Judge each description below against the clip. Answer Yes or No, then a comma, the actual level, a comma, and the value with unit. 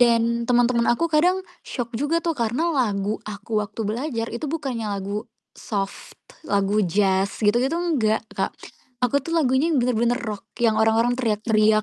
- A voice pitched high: Yes, high, 235 Hz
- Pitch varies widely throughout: No, average, 3.8 semitones